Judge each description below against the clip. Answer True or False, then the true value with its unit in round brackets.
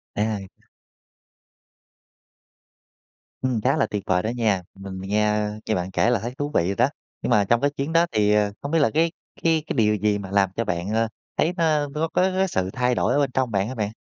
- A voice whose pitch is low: True (110 Hz)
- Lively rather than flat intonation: True (5.7 semitones)